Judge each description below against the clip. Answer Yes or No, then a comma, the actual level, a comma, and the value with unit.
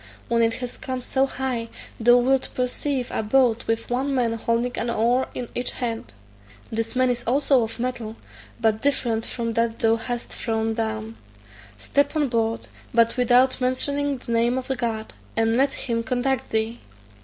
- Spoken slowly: No, average, 170 wpm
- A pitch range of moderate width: No, narrow, 2.2 semitones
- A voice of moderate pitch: No, high, 240 Hz